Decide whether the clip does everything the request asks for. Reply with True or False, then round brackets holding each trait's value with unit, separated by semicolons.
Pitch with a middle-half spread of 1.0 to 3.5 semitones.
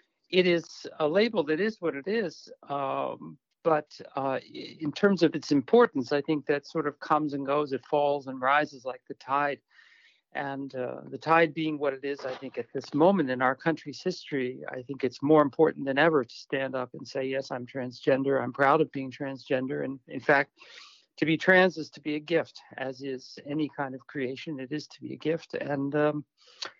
True (2.7 semitones)